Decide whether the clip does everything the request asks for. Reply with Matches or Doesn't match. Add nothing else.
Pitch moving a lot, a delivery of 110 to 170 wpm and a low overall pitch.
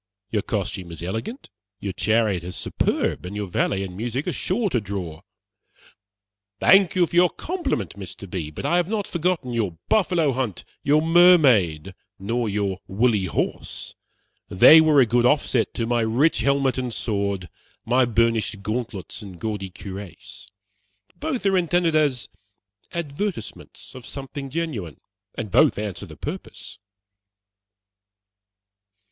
Matches